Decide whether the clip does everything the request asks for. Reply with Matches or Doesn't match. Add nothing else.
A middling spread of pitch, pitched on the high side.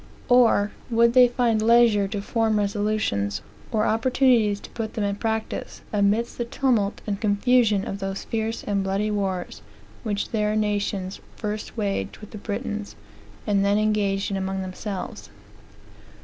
Doesn't match